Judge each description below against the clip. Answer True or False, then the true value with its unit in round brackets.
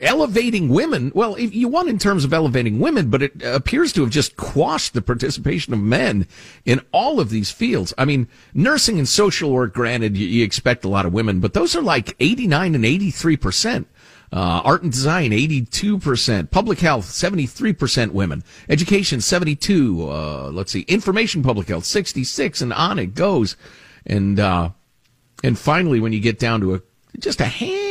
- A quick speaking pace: False (180 wpm)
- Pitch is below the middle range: True (130 Hz)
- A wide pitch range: True (7.9 semitones)